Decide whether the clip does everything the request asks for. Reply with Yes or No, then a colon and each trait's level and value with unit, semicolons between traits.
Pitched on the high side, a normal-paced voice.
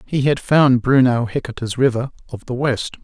No: low, 125 Hz; average, 180 wpm